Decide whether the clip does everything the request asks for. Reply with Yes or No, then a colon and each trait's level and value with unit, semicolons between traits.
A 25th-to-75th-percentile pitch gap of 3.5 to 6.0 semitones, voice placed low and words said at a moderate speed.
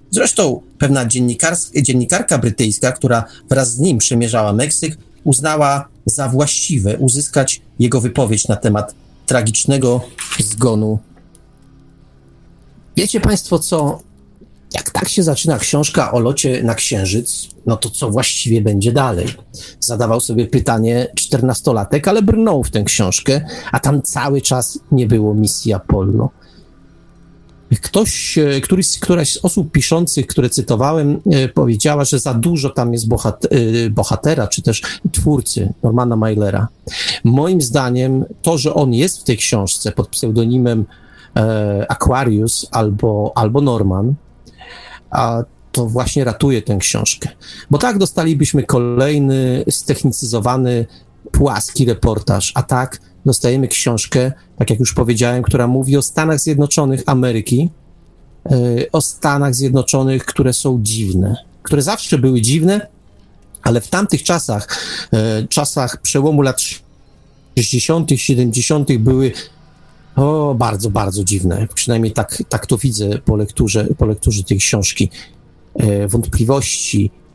Yes: average, 4.2 semitones; low, 125 Hz; average, 120 wpm